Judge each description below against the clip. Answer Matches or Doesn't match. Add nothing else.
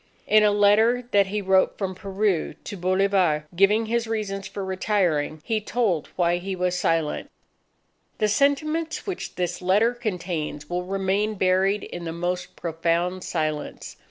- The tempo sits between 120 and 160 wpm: Matches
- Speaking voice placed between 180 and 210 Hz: Matches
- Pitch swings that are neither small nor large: Matches